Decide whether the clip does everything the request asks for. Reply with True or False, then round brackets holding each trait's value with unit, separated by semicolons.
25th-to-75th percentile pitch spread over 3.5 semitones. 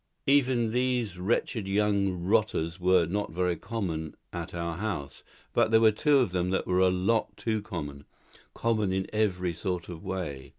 True (3.9 semitones)